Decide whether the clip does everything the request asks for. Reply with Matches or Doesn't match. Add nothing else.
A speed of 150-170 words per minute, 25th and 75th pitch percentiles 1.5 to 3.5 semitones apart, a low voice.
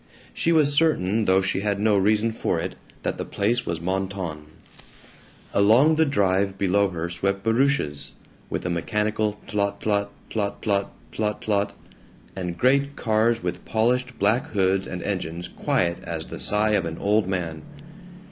Matches